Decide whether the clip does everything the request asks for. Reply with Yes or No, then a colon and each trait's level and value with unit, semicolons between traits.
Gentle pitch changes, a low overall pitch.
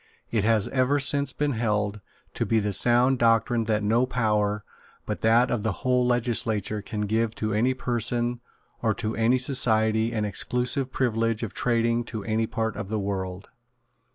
Yes: narrow, 2.3 semitones; low, 115 Hz